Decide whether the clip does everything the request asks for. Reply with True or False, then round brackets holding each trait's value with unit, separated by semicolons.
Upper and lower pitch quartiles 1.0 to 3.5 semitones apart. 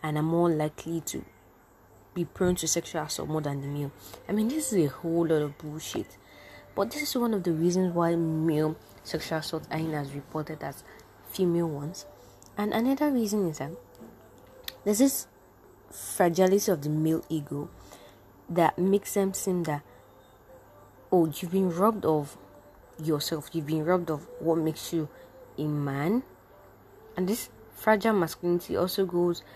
False (4.3 semitones)